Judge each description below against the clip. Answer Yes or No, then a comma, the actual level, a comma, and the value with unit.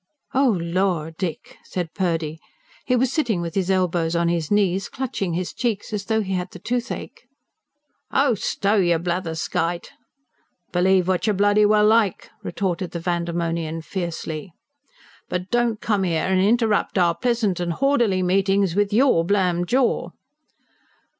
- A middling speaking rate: Yes, average, 145 wpm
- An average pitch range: Yes, average, 3.6 semitones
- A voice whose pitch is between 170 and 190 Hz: Yes, medium, 185 Hz